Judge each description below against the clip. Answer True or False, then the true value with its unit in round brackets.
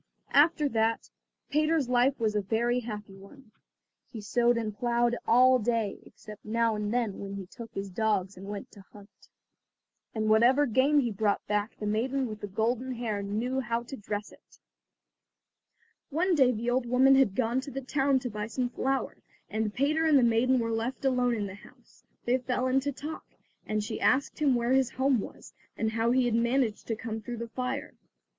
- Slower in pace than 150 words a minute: False (195 wpm)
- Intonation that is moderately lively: True (3.3 semitones)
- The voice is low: False (235 Hz)